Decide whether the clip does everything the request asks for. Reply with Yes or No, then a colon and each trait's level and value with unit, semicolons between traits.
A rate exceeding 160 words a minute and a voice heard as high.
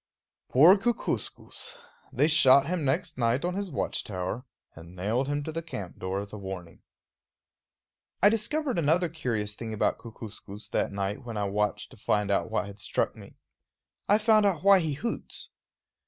No: average, 170 wpm; low, 130 Hz